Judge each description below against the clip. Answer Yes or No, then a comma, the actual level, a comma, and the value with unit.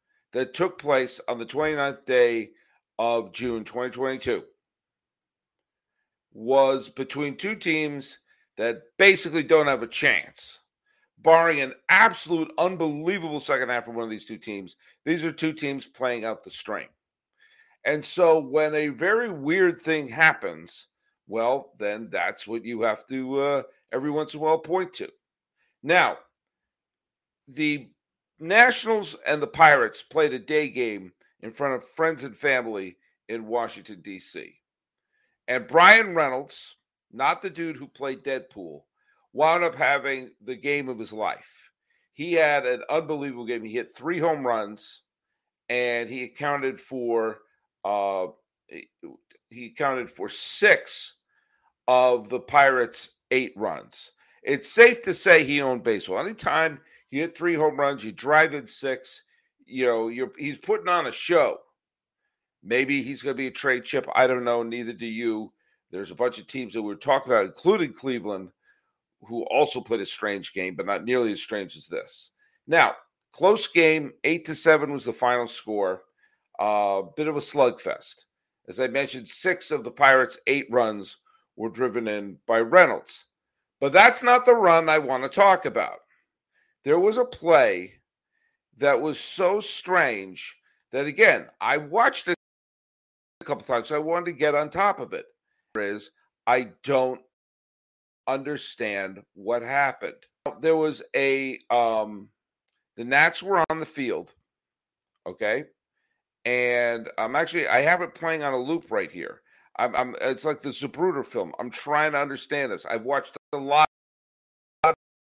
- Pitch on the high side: No, medium, 140 Hz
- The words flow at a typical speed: Yes, average, 155 wpm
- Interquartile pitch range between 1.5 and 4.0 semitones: No, wide, 5.6 semitones